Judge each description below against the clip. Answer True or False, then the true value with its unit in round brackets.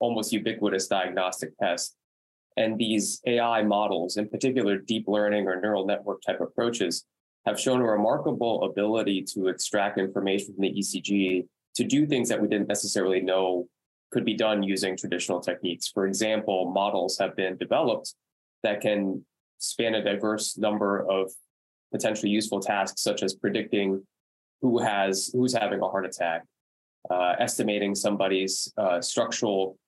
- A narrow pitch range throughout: True (2.2 semitones)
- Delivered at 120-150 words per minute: True (145 wpm)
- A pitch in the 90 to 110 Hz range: True (100 Hz)